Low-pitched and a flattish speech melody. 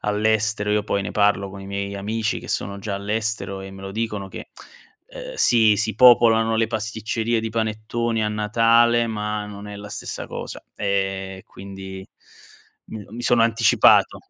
Yes: low, 105 Hz; narrow, 2.1 semitones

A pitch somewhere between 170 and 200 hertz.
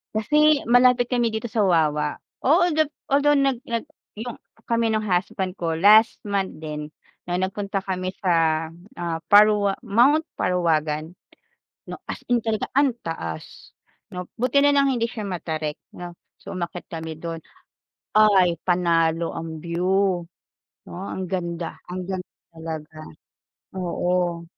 Yes: medium, 185 Hz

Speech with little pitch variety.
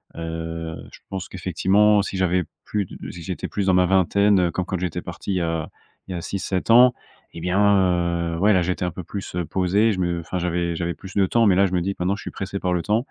Yes: narrow, 2.3 semitones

